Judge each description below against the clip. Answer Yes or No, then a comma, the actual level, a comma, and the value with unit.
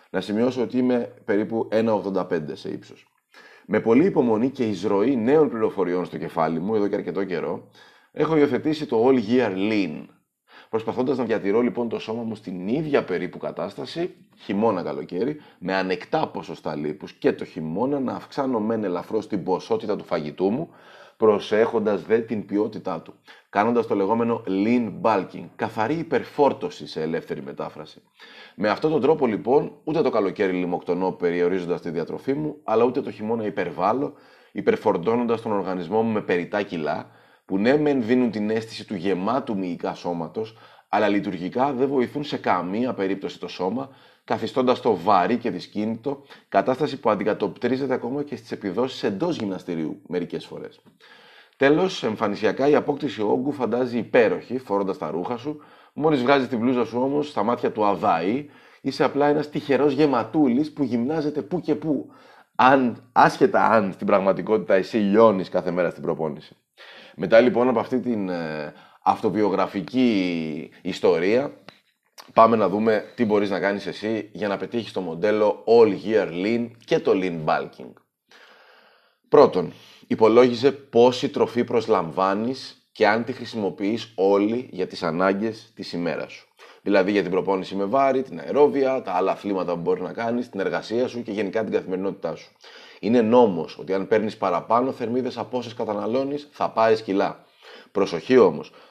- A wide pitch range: No, average, 4.8 semitones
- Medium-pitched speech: No, low, 115 Hz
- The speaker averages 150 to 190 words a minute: Yes, average, 155 wpm